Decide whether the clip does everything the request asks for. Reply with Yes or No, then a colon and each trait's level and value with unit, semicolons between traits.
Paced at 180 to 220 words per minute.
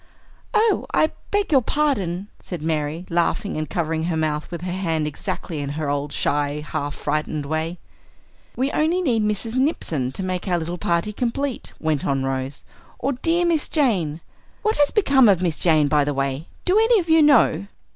Yes: average, 185 wpm